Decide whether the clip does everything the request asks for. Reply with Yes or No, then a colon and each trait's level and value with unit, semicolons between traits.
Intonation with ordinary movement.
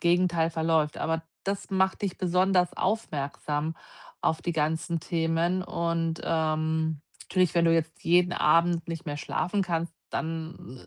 No: narrow, 1.8 semitones